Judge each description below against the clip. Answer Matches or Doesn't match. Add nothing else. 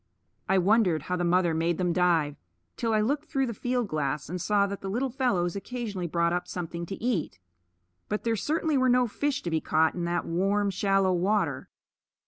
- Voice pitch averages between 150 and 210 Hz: Matches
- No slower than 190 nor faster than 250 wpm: Matches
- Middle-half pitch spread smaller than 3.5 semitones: Doesn't match